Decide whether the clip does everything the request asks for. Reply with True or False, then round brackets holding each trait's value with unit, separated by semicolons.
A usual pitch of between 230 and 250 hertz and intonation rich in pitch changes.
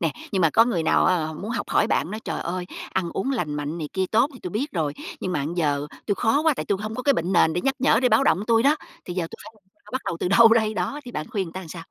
False (195 Hz; 5.7 semitones)